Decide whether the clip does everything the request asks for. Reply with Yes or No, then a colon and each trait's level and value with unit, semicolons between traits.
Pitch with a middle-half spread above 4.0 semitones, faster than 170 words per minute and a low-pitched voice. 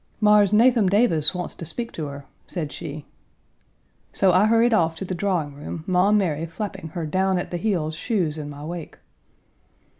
No: average, 4.7 semitones; average, 180 wpm; medium, 180 Hz